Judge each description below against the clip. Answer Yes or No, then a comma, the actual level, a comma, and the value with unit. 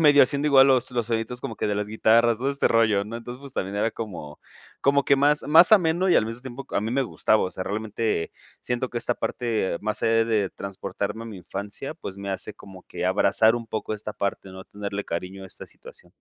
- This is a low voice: Yes, low, 115 Hz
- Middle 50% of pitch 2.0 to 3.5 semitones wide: No, average, 4.1 semitones